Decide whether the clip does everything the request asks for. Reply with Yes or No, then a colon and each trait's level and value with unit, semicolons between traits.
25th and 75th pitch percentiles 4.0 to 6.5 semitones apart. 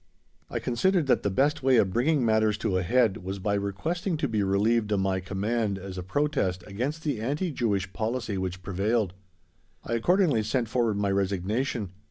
Yes: average, 4.7 semitones